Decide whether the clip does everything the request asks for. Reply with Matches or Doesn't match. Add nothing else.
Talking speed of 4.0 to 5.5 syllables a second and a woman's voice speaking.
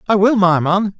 Doesn't match